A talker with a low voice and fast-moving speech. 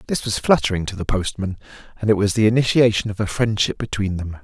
Yes: low, 105 Hz; fast, 215 wpm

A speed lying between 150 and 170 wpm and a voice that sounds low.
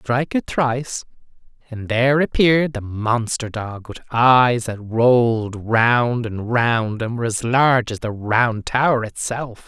Yes: average, 155 wpm; low, 120 Hz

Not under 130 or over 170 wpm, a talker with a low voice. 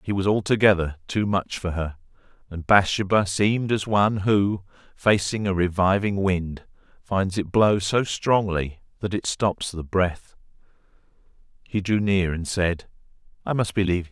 Yes: average, 155 wpm; very low, 95 Hz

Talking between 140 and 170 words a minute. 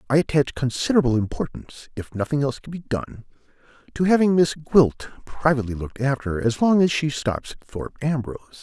Yes: average, 160 wpm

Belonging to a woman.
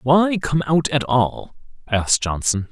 No: male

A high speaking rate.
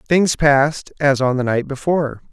No: average, 180 wpm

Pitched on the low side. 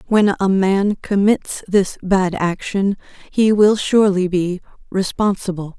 No: high, 195 Hz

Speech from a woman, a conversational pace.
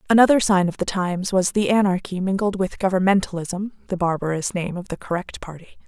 Yes: female; average, 185 wpm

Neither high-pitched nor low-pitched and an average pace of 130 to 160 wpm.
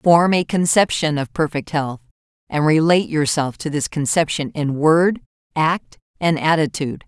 Yes: medium, 155 Hz; average, 145 wpm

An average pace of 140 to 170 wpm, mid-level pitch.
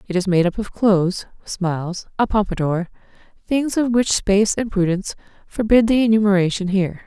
No: average, 160 wpm; high, 200 Hz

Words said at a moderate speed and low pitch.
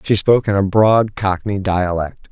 Yes: average, 180 wpm; low, 100 Hz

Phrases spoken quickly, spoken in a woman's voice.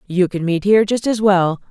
Yes: fast, 245 wpm; female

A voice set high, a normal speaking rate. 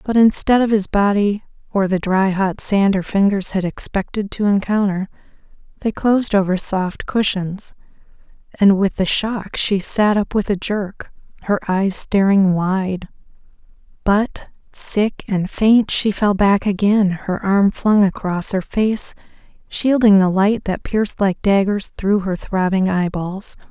Yes: high, 200 Hz; average, 155 wpm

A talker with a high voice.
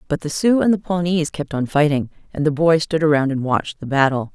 No: medium, 155 Hz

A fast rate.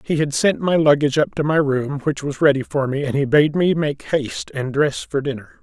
Yes: fast, 255 wpm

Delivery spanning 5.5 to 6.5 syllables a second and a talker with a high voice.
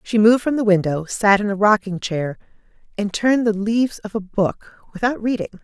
Yes: 5.7 syllables/s; high, 210 Hz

